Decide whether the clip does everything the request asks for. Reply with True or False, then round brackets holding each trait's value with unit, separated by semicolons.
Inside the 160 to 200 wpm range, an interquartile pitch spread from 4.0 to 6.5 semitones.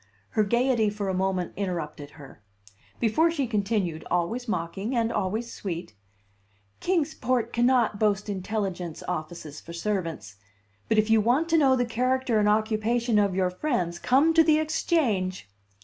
False (150 wpm; 5.1 semitones)